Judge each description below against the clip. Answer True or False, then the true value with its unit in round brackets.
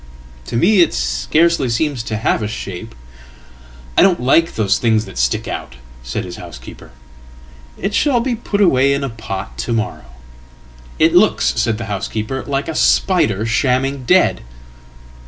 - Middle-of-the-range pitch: False (110 Hz)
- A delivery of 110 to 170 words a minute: True (145 wpm)